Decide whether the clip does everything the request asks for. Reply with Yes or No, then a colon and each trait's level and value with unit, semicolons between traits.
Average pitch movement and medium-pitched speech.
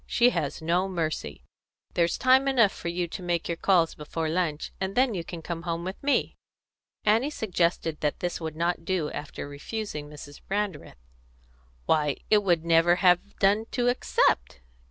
Yes: average, 4.1 semitones; medium, 175 Hz